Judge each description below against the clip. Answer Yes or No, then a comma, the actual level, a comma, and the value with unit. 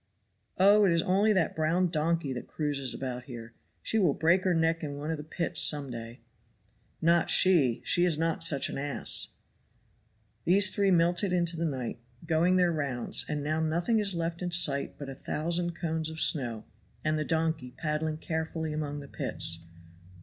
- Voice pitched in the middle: Yes, medium, 160 Hz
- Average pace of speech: Yes, average, 180 wpm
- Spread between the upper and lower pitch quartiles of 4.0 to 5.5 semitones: No, average, 3.1 semitones